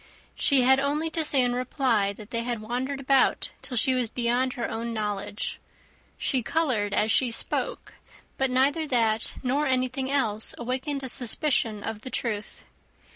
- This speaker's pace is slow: No, average, 165 wpm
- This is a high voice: Yes, very high, 250 Hz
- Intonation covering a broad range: No, average, 3.2 semitones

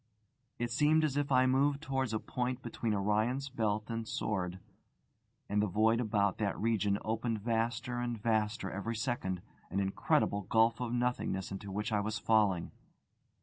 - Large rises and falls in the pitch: No, average, 3.0 semitones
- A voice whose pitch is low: Yes, low, 110 Hz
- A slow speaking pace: No, average, 160 wpm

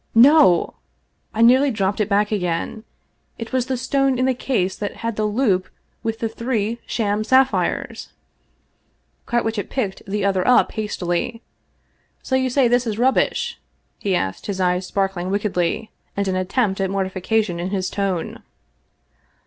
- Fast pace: No, average, 155 wpm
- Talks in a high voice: Yes, high, 210 Hz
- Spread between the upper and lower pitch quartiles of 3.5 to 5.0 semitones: Yes, average, 4.1 semitones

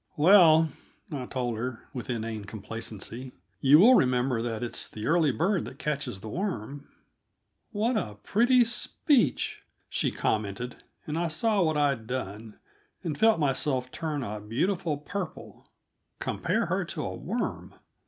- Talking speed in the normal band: Yes, average, 145 wpm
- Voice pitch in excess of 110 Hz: Yes, medium, 140 Hz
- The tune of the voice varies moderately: No, wide, 6.7 semitones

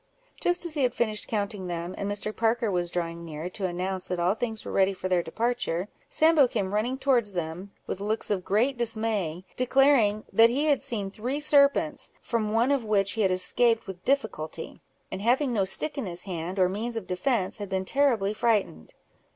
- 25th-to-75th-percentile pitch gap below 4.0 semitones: No, average, 4.6 semitones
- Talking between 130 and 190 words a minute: No, average, 200 wpm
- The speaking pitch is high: Yes, high, 210 Hz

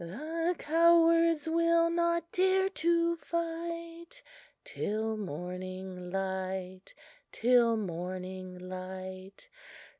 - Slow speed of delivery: Yes, slow, 80 wpm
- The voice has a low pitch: No, high, 245 Hz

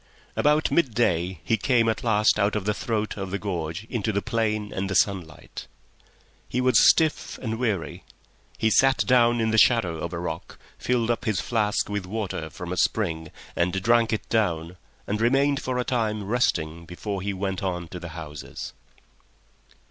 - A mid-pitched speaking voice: No, low, 105 Hz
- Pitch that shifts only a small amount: No, average, 4.5 semitones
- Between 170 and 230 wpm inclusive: Yes, average, 180 wpm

